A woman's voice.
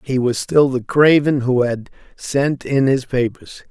No: male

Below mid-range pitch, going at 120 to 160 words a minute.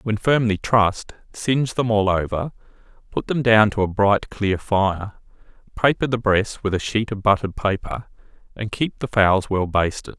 No: low, 105 Hz; average, 175 wpm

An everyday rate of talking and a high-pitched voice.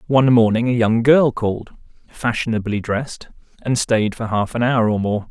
No: average, 180 wpm; low, 115 Hz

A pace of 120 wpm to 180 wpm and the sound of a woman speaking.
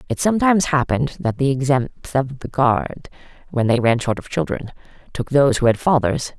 No: average, 190 wpm; female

